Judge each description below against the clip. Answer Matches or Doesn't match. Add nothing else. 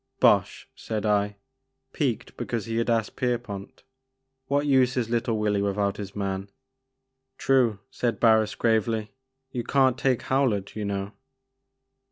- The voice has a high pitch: Doesn't match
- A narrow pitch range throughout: Doesn't match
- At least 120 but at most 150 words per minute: Matches